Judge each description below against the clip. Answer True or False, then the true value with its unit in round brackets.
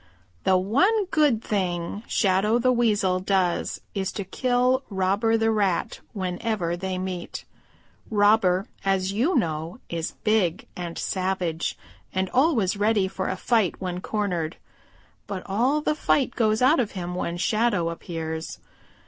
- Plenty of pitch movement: False (3.8 semitones)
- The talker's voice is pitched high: True (195 Hz)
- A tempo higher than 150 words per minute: False (140 wpm)